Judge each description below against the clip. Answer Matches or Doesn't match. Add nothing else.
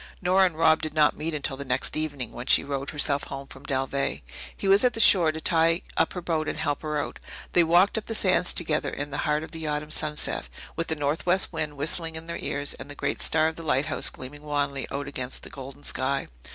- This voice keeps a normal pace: Doesn't match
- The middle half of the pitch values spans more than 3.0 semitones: Doesn't match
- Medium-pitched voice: Matches